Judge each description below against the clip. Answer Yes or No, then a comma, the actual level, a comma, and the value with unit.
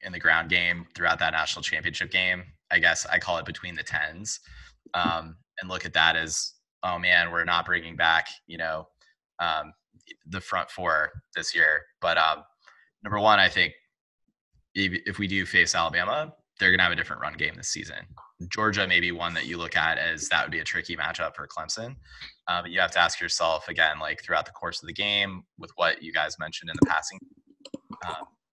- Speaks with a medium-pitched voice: No, very low, 90 Hz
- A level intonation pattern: No, average, 3.2 semitones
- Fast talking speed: Yes, fast, 210 wpm